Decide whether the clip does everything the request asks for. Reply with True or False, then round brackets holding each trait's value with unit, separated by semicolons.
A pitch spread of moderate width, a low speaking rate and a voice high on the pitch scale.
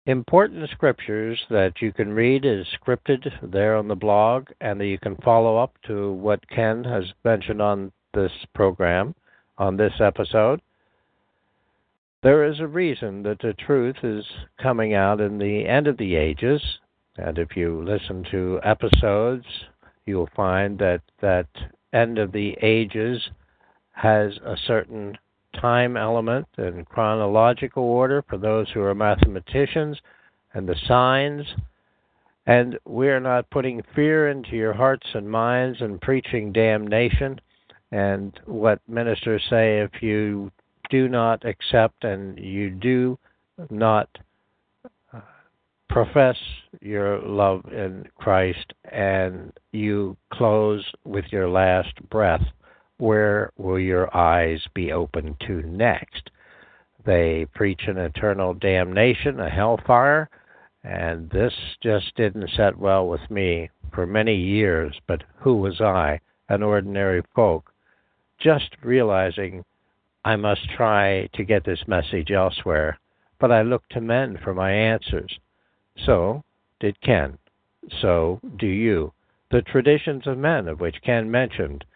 False (3.8 semitones; 130 wpm; 105 Hz)